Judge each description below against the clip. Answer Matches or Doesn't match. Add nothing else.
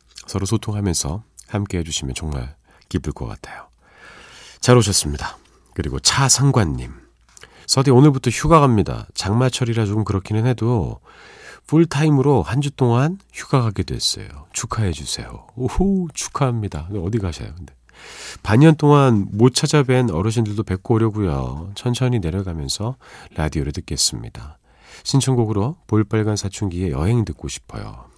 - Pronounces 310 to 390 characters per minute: Matches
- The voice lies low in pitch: Matches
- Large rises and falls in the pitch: Matches